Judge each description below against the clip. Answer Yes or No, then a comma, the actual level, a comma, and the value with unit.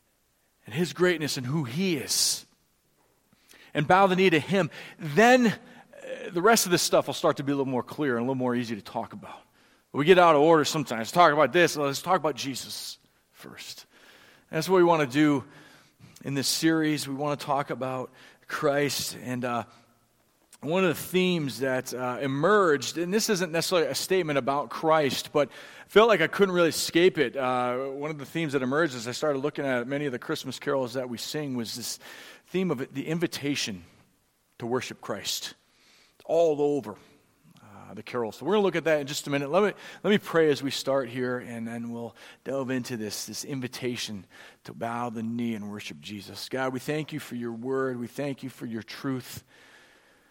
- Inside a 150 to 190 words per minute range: No, fast, 205 wpm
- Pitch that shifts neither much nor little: Yes, average, 4.8 semitones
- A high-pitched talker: No, medium, 140 Hz